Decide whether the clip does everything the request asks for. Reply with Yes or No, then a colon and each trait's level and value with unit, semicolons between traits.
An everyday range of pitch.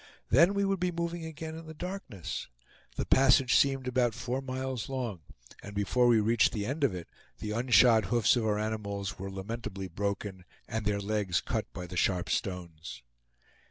Yes: average, 5.0 semitones